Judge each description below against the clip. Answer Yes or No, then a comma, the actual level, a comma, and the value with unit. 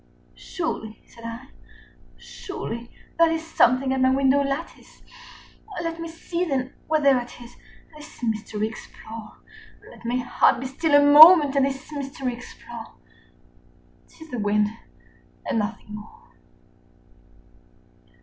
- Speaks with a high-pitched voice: Yes, very high, 270 Hz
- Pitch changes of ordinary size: Yes, average, 4.8 semitones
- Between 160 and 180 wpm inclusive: No, slow, 135 wpm